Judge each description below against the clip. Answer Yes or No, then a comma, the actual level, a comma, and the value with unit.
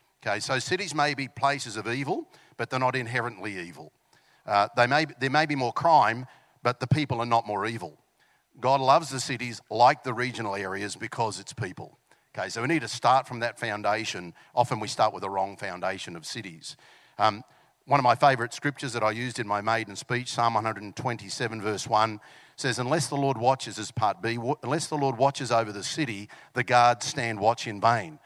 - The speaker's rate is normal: No, fast, 210 wpm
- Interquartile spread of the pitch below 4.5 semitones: Yes, average, 3.8 semitones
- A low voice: Yes, low, 120 Hz